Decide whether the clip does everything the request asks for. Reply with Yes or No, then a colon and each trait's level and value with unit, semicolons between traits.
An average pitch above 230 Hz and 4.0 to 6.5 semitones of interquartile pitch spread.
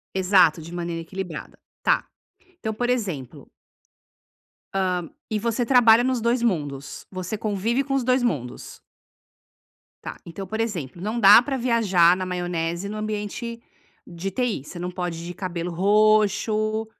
No: high, 200 Hz; average, 4.6 semitones